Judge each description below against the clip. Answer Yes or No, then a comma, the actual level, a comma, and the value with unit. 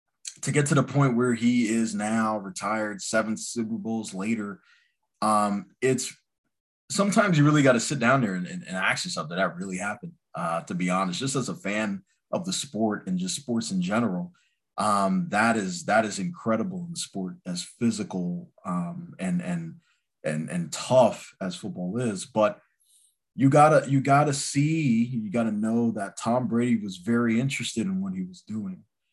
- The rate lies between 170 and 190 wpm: Yes, average, 185 wpm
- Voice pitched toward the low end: Yes, low, 120 Hz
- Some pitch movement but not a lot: No, wide, 8.0 semitones